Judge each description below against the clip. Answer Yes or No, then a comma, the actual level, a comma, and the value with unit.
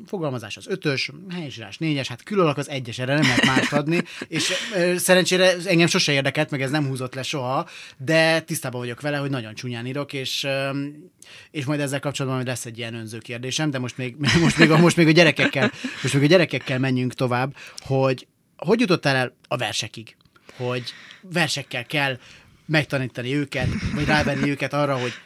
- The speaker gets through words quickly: Yes, fast, 190 wpm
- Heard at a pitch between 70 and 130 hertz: No, medium, 140 Hz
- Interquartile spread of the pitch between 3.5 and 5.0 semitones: Yes, average, 3.8 semitones